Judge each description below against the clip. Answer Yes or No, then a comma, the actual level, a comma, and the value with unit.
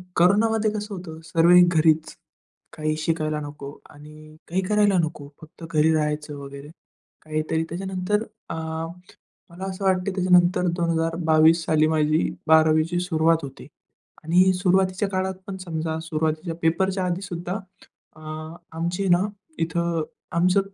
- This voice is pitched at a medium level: Yes, medium, 170 Hz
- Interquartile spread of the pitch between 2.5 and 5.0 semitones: Yes, average, 2.8 semitones